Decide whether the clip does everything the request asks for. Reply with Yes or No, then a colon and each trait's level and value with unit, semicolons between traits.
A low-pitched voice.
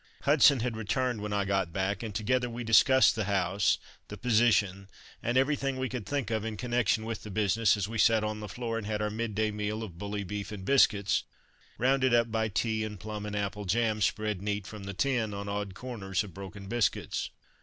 Yes: low, 110 Hz